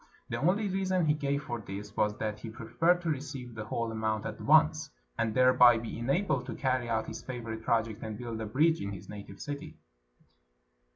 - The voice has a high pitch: No, low, 120 Hz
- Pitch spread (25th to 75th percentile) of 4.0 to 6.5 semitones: Yes, average, 5.2 semitones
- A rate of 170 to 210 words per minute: Yes, average, 195 wpm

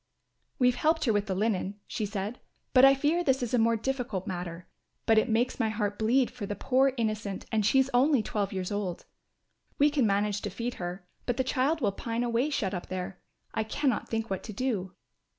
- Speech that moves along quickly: Yes, fast, 210 wpm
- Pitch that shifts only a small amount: No, average, 4.2 semitones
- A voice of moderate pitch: No, high, 225 Hz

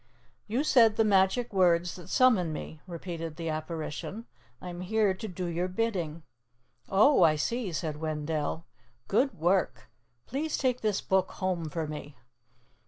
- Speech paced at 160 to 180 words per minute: No, average, 150 wpm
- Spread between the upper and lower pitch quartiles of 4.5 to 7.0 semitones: Yes, average, 5.0 semitones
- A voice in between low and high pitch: Yes, medium, 180 Hz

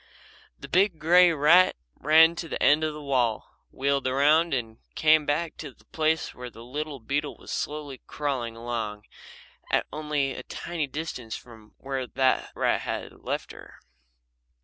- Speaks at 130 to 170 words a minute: Yes, average, 160 wpm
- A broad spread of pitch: No, average, 3.7 semitones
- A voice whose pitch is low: No, medium, 145 Hz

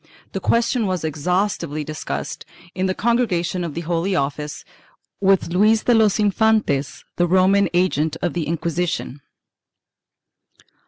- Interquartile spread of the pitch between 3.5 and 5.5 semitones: Yes, average, 4.2 semitones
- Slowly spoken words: Yes, slow, 130 wpm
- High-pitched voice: No, medium, 180 Hz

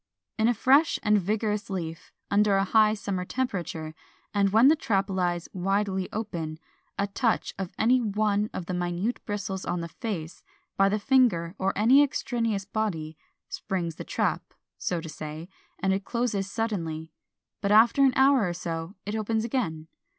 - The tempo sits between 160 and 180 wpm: Yes, average, 165 wpm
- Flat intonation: No, average, 3.9 semitones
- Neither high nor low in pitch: No, high, 200 Hz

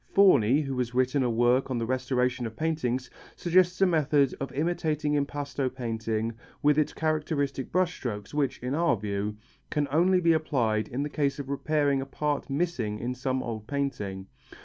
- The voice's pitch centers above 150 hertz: No, low, 135 Hz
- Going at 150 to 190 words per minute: Yes, average, 175 wpm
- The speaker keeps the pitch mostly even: No, average, 3.9 semitones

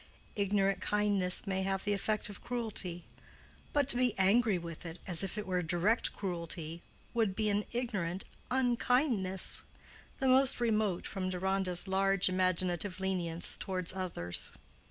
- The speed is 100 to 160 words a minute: Yes, average, 140 wpm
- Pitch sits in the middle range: No, high, 195 Hz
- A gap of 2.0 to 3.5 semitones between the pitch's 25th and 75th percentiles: Yes, average, 2.9 semitones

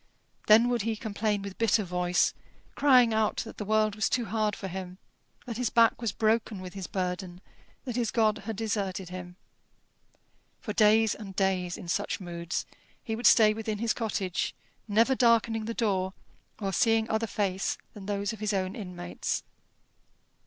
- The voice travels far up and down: No, average, 2.9 semitones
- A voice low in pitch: No, high, 210 Hz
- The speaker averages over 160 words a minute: Yes, average, 170 wpm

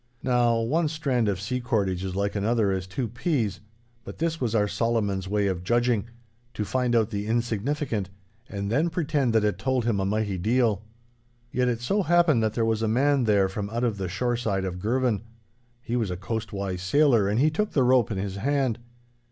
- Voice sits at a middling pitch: No, low, 115 Hz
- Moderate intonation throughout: Yes, average, 3.9 semitones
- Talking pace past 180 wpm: Yes, average, 200 wpm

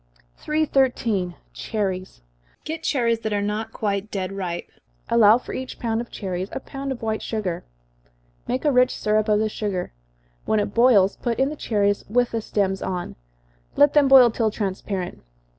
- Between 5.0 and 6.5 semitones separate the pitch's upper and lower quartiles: No, average, 3.8 semitones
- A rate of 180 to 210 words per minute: No, average, 170 wpm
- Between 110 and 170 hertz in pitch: No, high, 215 Hz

